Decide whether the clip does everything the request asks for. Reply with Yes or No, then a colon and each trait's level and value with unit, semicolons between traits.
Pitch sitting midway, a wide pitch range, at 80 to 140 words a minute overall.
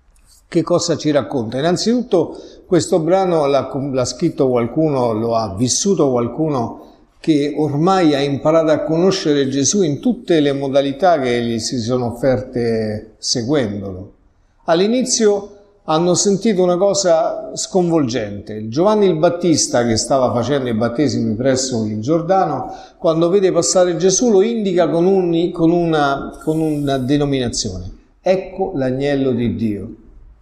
Yes: medium, 145 Hz; wide, 6.6 semitones; average, 130 wpm